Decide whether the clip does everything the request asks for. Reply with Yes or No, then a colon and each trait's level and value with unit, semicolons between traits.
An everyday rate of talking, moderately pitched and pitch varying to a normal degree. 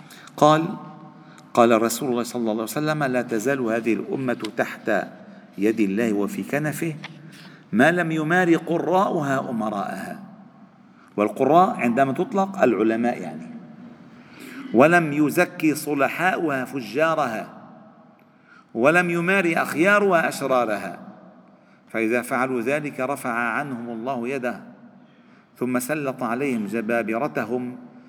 No: average, 100 wpm; medium, 150 Hz; wide, 8.8 semitones